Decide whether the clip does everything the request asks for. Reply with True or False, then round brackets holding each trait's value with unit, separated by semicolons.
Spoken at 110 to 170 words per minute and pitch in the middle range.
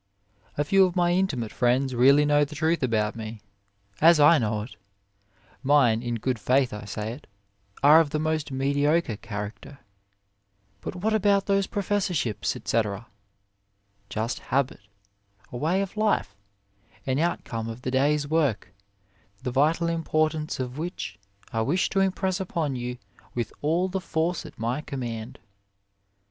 True (160 wpm; 145 Hz)